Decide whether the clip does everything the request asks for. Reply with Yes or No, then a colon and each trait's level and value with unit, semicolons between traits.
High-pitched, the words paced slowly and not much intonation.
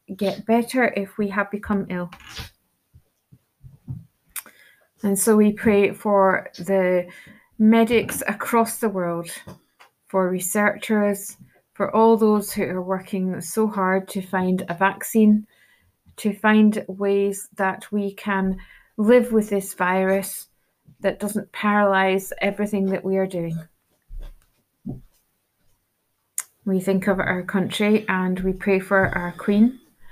Yes: high, 200 Hz; slow, 120 wpm; narrow, 1.8 semitones